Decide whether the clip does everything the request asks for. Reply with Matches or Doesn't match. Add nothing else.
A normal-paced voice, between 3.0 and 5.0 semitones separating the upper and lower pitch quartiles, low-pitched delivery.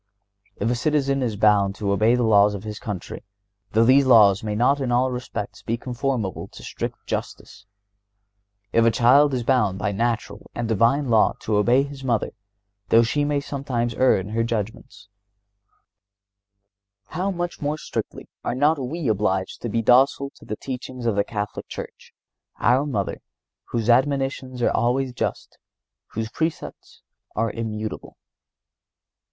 Matches